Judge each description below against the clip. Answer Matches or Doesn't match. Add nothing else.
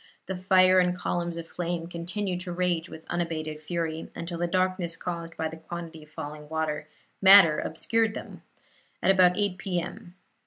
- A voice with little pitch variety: Matches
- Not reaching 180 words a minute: Matches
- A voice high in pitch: Doesn't match